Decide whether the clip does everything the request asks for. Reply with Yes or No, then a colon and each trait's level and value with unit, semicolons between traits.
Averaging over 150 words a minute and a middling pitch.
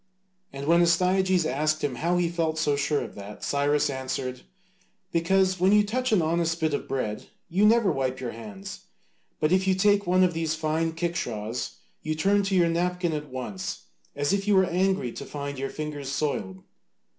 Yes: average, 190 wpm; medium, 160 Hz